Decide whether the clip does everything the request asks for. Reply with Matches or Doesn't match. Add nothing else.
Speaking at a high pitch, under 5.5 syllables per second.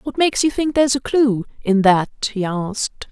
Matches